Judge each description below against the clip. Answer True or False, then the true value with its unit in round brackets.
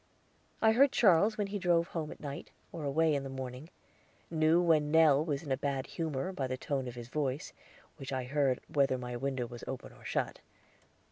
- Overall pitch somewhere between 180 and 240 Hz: False (145 Hz)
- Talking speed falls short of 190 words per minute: False (205 wpm)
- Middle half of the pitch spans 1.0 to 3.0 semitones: False (3.6 semitones)